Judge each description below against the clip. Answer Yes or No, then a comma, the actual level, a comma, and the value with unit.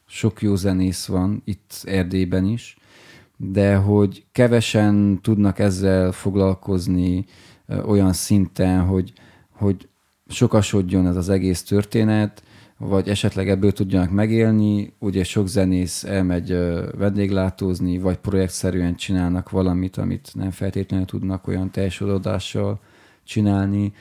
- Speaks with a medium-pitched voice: No, very low, 95 Hz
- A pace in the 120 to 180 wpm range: No, slow, 105 wpm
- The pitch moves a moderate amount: No, narrow, 1.7 semitones